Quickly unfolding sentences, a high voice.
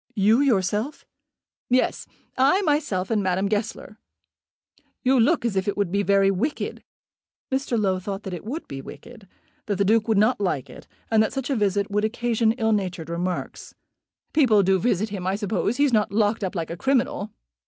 No: average, 185 wpm; high, 210 Hz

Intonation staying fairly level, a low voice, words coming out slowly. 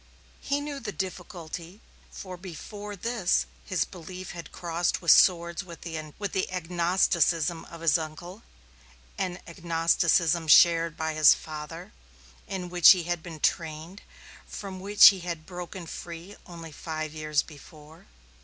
No: narrow, 2.3 semitones; medium, 170 Hz; slow, 130 wpm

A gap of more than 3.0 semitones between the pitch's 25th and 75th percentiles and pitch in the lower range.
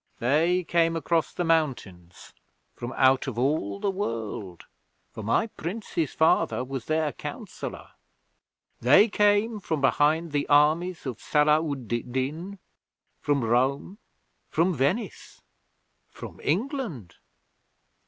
No: average, 5.3 semitones; medium, 150 Hz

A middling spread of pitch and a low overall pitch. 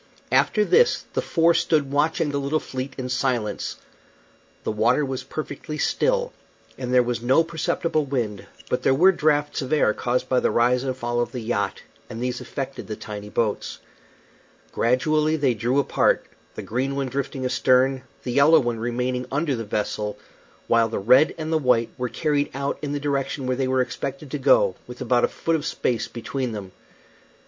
Yes: average, 3.4 semitones; low, 130 Hz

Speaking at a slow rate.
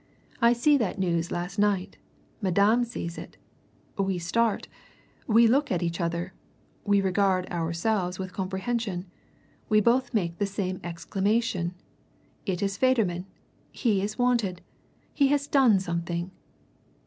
Yes: slow, 130 wpm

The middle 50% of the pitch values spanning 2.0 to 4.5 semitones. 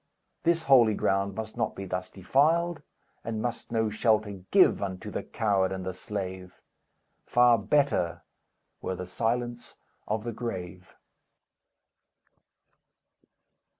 Yes: average, 4.2 semitones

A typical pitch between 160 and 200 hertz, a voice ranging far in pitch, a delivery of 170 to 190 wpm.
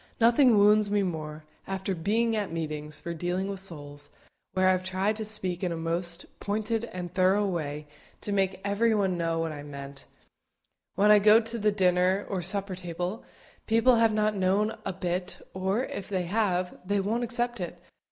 No: high, 190 Hz; average, 3.2 semitones; average, 180 wpm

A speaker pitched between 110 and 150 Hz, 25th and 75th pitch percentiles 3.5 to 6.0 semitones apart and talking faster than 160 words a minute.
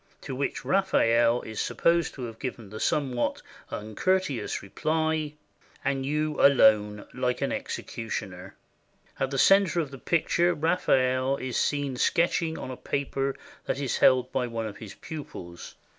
No: low, 135 Hz; average, 4.8 semitones; average, 145 wpm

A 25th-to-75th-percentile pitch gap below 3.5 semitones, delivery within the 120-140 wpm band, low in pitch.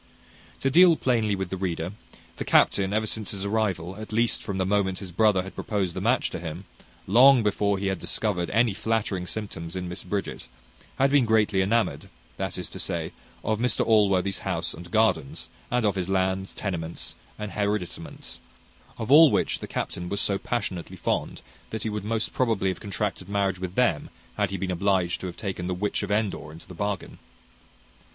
No: average, 2.8 semitones; average, 190 wpm; low, 100 Hz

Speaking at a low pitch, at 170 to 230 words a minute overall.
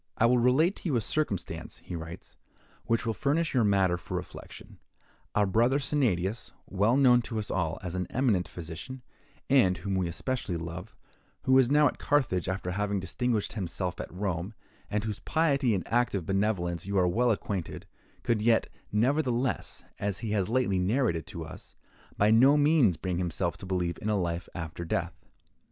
Yes: low, 105 Hz; average, 180 wpm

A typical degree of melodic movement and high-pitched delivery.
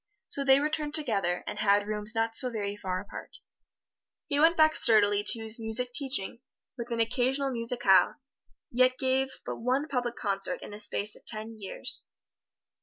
Yes: average, 4.2 semitones; high, 230 Hz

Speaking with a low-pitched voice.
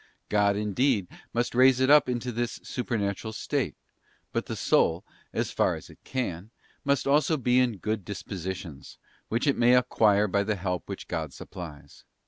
Yes: low, 110 Hz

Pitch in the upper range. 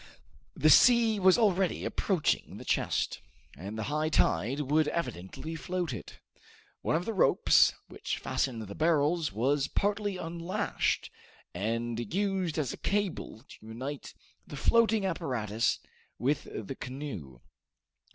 No: medium, 150 Hz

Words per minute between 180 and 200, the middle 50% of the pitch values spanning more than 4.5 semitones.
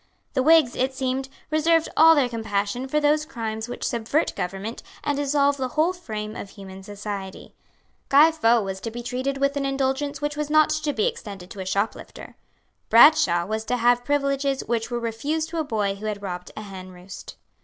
Yes: average, 190 wpm; wide, 5.6 semitones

